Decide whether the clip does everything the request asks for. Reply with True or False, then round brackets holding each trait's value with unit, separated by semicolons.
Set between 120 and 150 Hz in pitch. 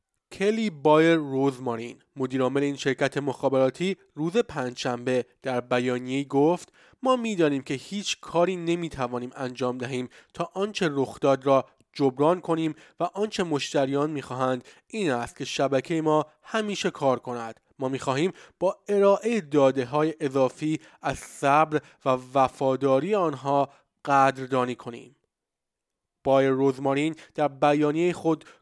True (140 Hz)